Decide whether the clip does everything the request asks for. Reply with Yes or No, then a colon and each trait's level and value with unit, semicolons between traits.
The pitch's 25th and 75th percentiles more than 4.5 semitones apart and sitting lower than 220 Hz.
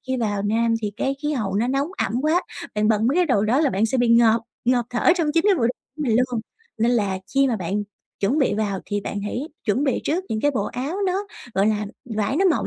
No: average, 4.9 semitones; high, 235 Hz